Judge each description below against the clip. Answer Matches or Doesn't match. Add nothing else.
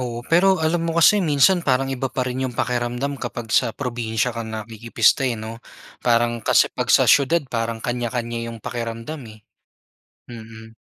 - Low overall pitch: Matches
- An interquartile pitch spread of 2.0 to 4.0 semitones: Matches